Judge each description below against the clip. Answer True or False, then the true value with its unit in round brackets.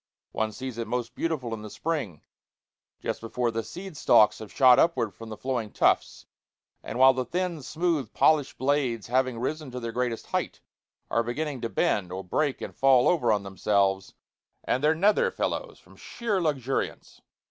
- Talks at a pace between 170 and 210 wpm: True (175 wpm)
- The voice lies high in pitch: False (125 Hz)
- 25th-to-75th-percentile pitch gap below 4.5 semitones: False (4.9 semitones)